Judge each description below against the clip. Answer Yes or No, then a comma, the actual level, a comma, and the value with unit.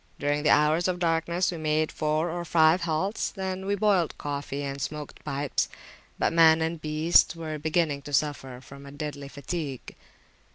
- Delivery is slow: No, average, 170 wpm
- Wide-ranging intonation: No, average, 2.8 semitones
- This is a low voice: No, medium, 155 Hz